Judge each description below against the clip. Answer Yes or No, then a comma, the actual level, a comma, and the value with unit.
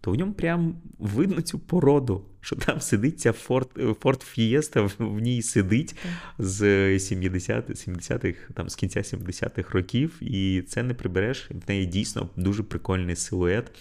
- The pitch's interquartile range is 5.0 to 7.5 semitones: Yes, wide, 5.5 semitones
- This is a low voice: Yes, low, 115 Hz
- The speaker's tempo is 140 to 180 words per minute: Yes, average, 150 wpm